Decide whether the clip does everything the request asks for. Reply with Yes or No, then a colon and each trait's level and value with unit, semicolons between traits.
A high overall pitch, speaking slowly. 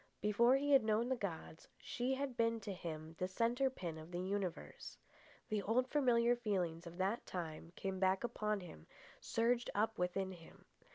No: high, 205 Hz; average, 175 wpm